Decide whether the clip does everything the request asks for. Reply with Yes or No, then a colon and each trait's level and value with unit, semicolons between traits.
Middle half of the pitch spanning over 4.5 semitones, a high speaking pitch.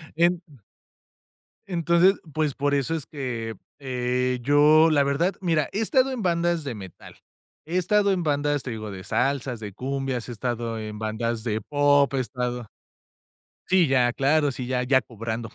No: average, 5.2 semitones; medium, 140 Hz